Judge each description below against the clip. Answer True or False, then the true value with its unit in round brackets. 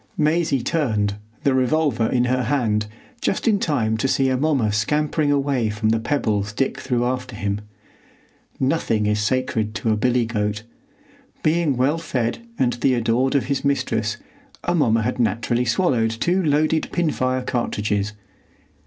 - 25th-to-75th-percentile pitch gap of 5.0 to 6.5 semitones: False (4.6 semitones)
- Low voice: True (125 Hz)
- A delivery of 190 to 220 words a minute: False (150 wpm)